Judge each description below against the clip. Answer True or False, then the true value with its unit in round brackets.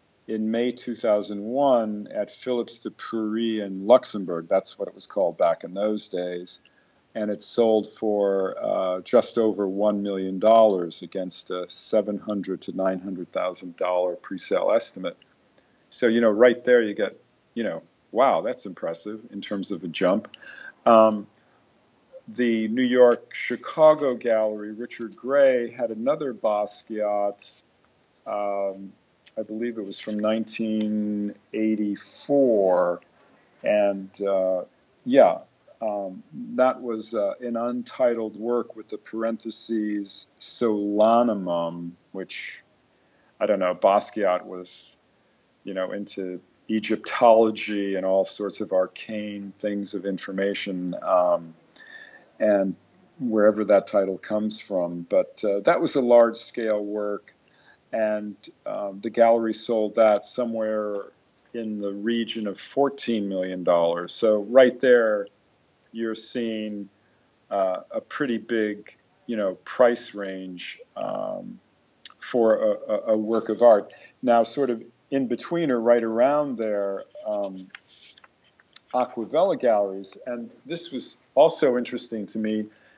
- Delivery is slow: True (125 wpm)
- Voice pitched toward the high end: False (110 Hz)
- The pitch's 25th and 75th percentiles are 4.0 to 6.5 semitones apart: False (2.9 semitones)